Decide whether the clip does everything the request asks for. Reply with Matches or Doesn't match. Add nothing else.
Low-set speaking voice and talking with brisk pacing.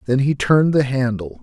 Matches